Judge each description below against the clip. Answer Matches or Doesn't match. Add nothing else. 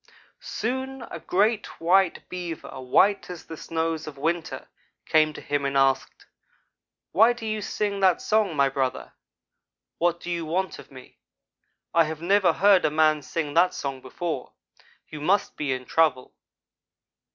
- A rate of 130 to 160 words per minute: Matches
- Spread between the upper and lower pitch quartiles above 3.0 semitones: Matches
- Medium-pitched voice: Matches